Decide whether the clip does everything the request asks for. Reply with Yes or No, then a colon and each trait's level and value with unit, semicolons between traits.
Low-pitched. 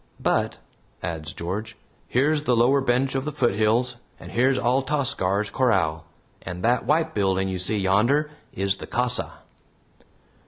Yes: low, 120 Hz